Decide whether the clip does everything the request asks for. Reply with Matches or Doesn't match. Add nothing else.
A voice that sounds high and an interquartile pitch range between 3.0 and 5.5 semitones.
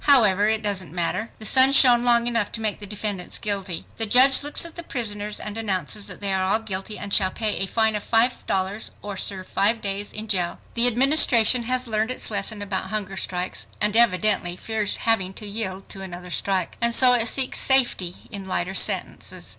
Matches